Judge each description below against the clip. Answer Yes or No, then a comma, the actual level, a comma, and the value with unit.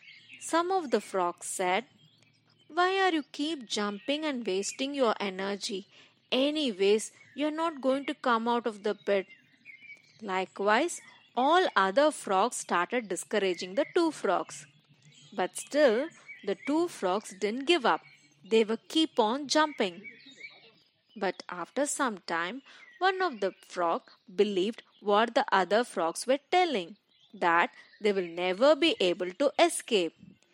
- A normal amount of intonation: No, wide, 7.3 semitones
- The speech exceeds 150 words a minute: No, average, 140 wpm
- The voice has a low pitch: No, high, 225 Hz